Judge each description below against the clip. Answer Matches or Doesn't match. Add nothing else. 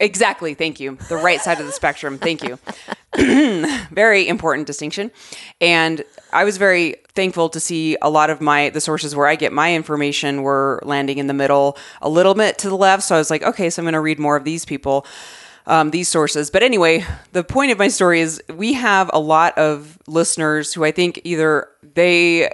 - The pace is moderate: Doesn't match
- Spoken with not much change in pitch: Doesn't match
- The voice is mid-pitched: Matches